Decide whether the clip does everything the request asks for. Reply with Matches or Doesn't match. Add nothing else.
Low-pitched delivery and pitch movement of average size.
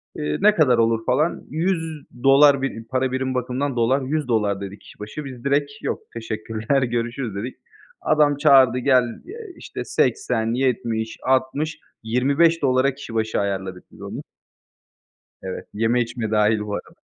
Matches